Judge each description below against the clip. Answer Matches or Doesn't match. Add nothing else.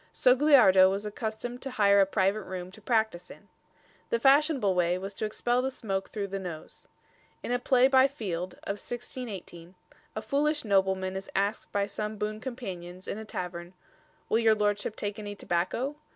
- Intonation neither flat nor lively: Matches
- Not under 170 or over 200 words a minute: Matches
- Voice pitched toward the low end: Doesn't match